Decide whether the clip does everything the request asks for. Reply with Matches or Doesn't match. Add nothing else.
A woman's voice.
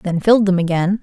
Matches